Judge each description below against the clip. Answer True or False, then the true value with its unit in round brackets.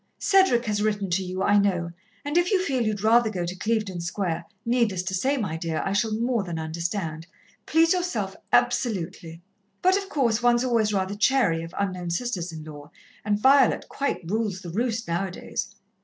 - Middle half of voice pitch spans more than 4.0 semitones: True (5.5 semitones)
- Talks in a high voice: True (205 Hz)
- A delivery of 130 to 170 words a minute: False (190 wpm)